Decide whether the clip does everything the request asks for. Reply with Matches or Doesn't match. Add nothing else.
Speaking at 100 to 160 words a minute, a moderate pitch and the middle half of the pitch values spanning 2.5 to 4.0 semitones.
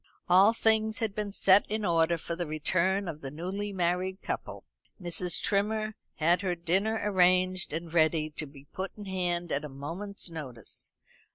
Doesn't match